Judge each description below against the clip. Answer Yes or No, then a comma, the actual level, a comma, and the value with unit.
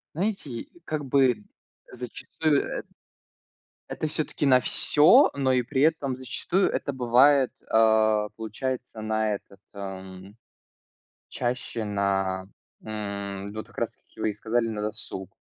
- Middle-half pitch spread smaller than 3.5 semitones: No, average, 4.3 semitones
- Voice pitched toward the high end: No, low, 115 Hz